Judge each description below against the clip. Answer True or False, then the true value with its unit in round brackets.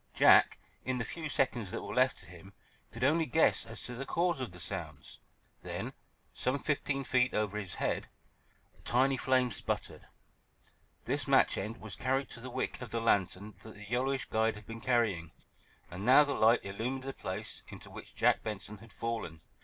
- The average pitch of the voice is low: True (115 Hz)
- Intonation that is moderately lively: True (4.1 semitones)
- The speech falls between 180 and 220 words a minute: True (190 wpm)